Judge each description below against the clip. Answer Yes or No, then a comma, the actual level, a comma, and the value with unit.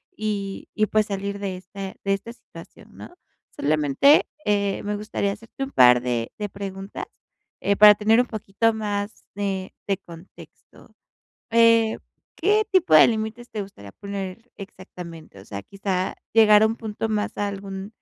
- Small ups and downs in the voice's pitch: Yes, narrow, 2.2 semitones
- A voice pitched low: No, high, 200 Hz